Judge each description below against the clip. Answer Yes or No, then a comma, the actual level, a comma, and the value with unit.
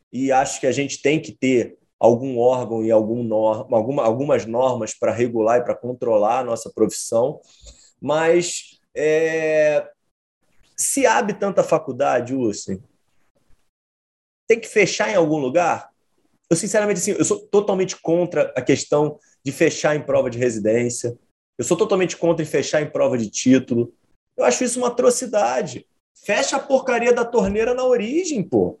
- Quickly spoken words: No, average, 150 wpm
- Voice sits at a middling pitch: Yes, medium, 155 Hz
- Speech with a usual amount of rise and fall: No, wide, 8.6 semitones